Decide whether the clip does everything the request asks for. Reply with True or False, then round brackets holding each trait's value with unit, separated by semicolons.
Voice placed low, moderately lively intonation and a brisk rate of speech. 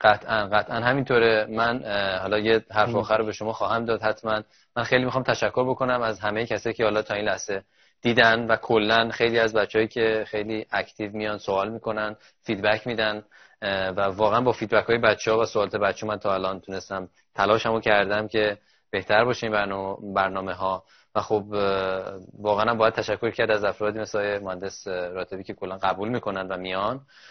False (105 Hz; 2.0 semitones; 175 wpm)